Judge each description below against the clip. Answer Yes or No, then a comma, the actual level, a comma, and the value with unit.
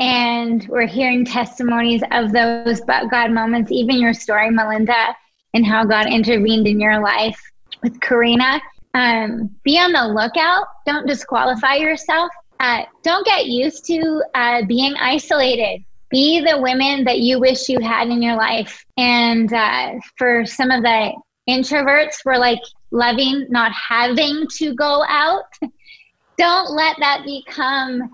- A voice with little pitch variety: No, average, 3.8 semitones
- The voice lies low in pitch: No, very high, 250 Hz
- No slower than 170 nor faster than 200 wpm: No, average, 145 wpm